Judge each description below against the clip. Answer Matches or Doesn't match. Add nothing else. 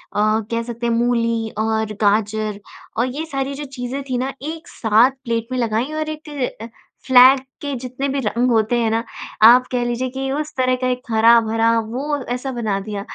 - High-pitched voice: Matches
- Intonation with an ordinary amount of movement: Matches